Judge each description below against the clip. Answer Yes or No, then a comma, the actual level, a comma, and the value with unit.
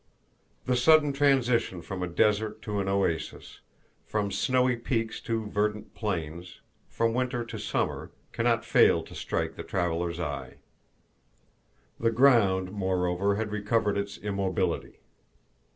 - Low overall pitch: Yes, low, 105 Hz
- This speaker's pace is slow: Yes, slow, 130 wpm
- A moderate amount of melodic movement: Yes, average, 3.7 semitones